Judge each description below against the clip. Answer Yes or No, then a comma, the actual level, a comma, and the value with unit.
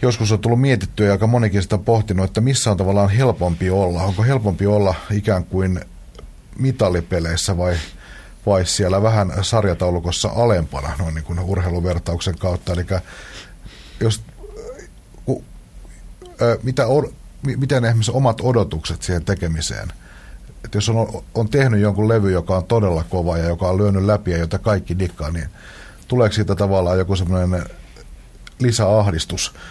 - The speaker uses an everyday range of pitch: Yes, average, 3.9 semitones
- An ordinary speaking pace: Yes, average, 140 wpm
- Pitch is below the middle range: Yes, low, 100 Hz